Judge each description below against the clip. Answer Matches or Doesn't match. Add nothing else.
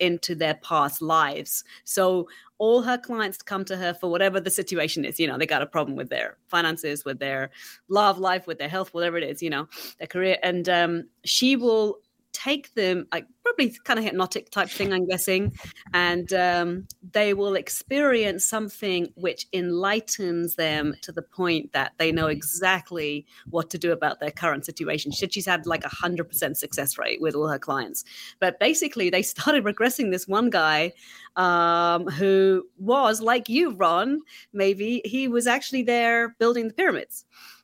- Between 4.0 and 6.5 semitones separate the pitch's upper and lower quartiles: Matches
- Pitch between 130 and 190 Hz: Matches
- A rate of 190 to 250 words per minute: Doesn't match